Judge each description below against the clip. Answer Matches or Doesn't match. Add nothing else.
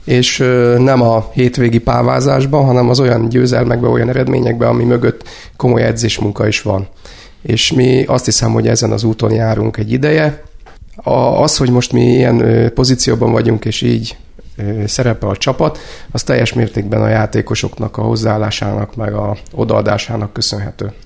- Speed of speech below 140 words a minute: Doesn't match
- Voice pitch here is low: Matches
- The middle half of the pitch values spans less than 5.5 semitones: Matches